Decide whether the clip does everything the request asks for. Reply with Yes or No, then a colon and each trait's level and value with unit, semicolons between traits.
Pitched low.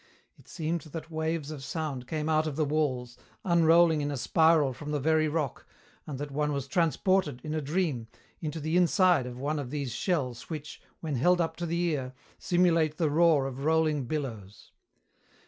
No: medium, 155 Hz